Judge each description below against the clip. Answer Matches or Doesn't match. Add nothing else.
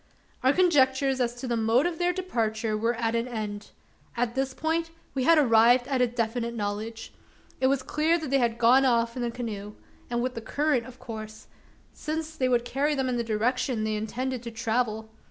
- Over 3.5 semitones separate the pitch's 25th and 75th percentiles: Doesn't match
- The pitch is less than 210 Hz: Doesn't match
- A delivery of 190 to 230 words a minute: Matches